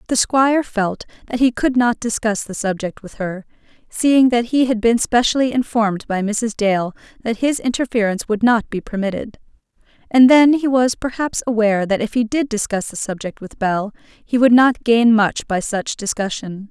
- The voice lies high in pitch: Yes, high, 225 Hz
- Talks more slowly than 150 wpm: No, average, 190 wpm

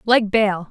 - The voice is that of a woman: Yes, female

